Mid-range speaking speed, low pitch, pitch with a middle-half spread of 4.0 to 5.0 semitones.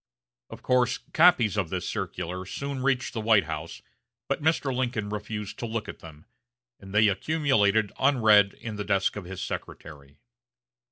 Yes: average, 160 wpm; low, 105 Hz; average, 4.7 semitones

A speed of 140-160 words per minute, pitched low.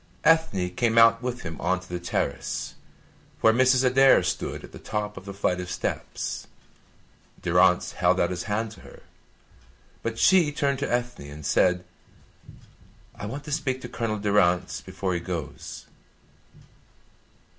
Yes: average, 155 wpm; low, 105 Hz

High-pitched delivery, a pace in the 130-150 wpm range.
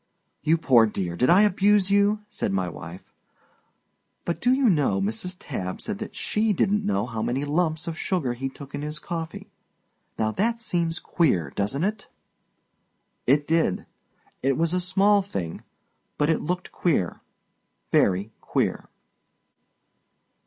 No: medium, 160 Hz; average, 145 wpm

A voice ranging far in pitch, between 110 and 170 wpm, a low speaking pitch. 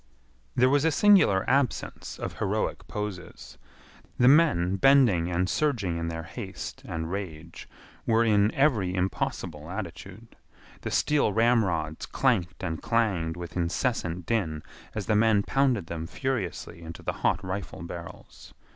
Yes: wide, 5.8 semitones; average, 140 wpm; very low, 95 Hz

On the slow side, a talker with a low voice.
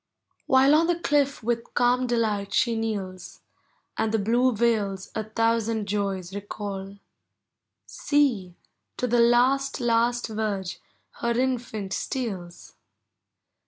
No: slow, 115 wpm; high, 230 Hz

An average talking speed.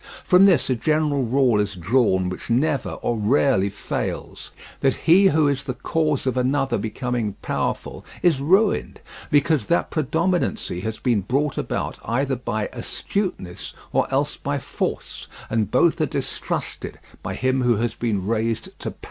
Yes: average, 155 wpm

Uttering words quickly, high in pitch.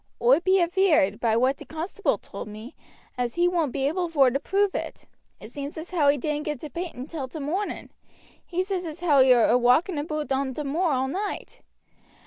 Yes: fast, 210 wpm; very high, 300 Hz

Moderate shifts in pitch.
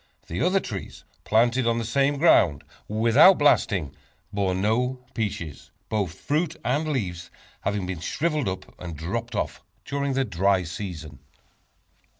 No: wide, 7.0 semitones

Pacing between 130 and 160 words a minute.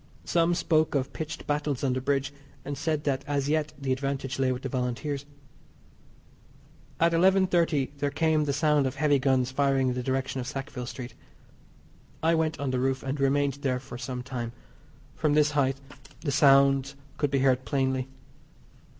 No: average, 175 wpm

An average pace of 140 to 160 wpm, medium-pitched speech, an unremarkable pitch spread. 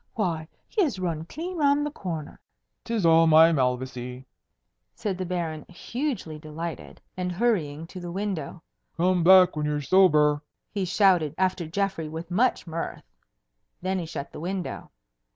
Yes: average, 150 wpm; medium, 175 Hz; average, 3.5 semitones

